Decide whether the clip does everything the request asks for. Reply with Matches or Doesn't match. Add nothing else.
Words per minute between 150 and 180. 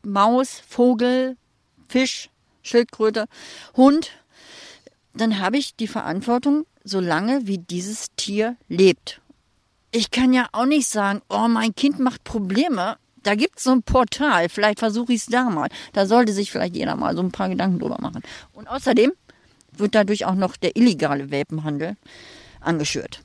Matches